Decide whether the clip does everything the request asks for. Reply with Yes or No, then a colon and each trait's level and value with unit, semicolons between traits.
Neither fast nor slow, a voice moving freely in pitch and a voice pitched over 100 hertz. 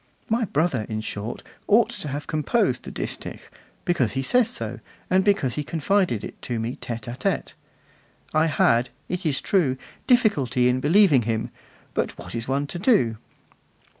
Yes: average, 165 wpm; wide, 7.7 semitones; medium, 140 Hz